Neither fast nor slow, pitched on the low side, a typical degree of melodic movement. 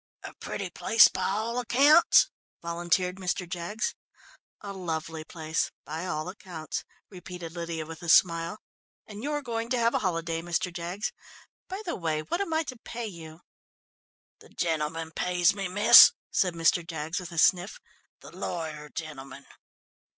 No: average, 155 wpm; medium, 175 Hz; average, 4.1 semitones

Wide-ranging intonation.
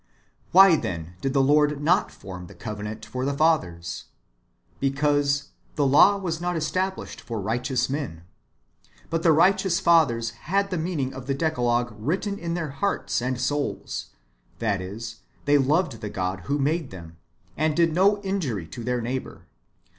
Yes: wide, 6.1 semitones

